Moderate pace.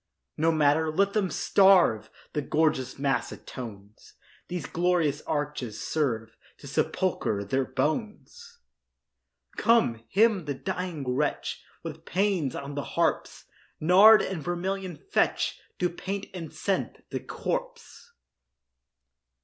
No: slow, 110 wpm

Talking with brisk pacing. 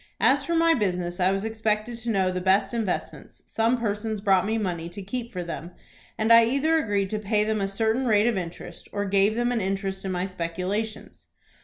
Yes: fast, 210 wpm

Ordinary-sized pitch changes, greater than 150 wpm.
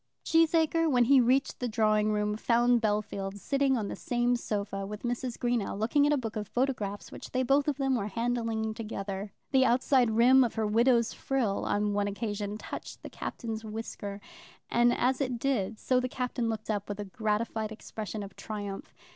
Yes: average, 3.2 semitones; average, 190 wpm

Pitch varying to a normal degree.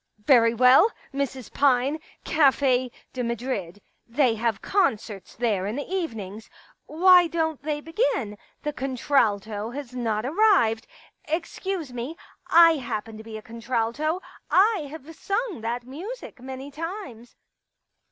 No: wide, 5.8 semitones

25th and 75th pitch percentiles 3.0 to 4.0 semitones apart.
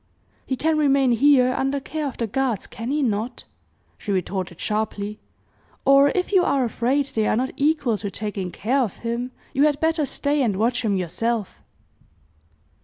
No: average, 4.7 semitones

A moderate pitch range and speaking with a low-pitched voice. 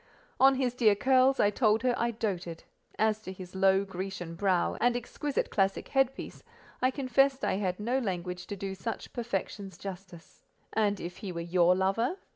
No: average, 4.7 semitones; high, 205 Hz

